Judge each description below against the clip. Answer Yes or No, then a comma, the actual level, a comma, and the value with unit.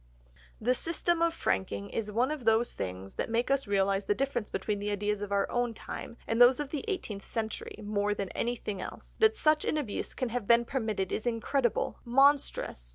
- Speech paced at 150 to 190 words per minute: No, average, 200 wpm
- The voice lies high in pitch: Yes, high, 230 Hz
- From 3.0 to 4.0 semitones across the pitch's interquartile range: No, average, 4.6 semitones